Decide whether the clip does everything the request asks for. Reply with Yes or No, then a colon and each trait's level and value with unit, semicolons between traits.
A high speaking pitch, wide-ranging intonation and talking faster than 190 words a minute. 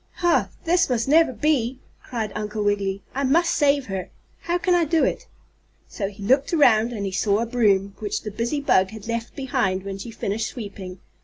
Yes: high, 225 Hz; wide, 5.7 semitones; average, 200 wpm